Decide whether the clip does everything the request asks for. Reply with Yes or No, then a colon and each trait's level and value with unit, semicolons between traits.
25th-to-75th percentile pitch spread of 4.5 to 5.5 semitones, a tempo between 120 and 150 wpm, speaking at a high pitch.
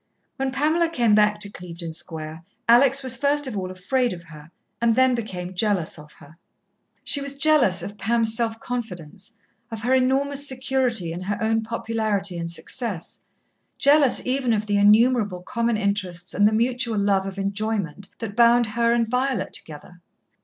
No: average, 4.9 semitones; average, 165 wpm; high, 220 Hz